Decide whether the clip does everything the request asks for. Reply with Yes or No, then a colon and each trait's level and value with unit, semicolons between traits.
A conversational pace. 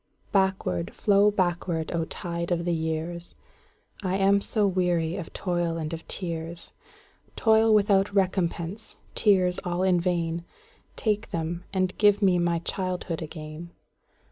No: slow, 120 wpm